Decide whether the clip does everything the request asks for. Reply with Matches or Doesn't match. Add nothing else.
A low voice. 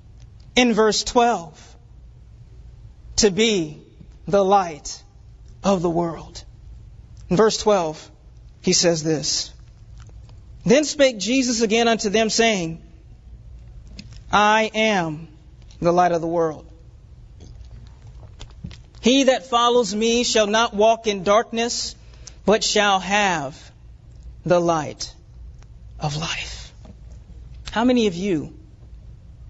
Doesn't match